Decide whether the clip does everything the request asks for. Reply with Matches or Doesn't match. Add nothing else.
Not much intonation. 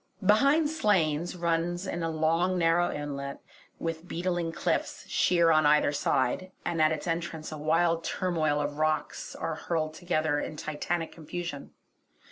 Matches